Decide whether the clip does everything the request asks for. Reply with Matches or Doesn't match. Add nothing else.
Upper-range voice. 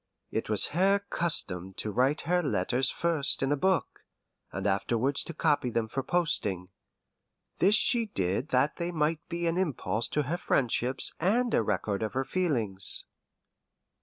Doesn't match